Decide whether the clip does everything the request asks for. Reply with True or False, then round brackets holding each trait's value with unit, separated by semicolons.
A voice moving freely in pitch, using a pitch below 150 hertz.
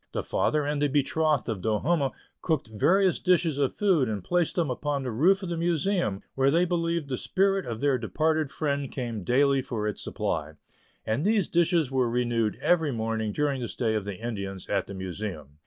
True (6.7 semitones; 140 Hz)